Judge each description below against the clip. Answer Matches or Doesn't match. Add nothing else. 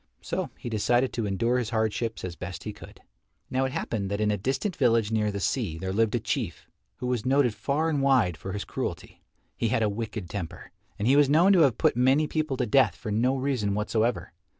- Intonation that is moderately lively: Matches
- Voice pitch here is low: Matches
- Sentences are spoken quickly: Matches